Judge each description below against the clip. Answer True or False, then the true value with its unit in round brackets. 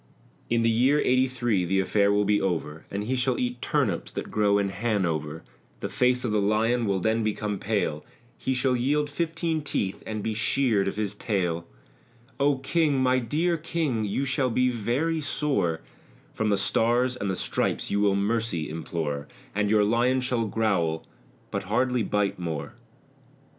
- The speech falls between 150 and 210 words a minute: True (175 wpm)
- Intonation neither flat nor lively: True (4.4 semitones)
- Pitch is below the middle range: True (110 Hz)